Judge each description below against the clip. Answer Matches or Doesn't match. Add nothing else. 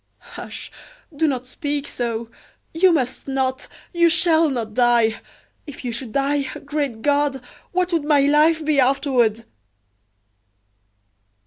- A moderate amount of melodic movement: Matches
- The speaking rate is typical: Doesn't match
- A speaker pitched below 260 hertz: Doesn't match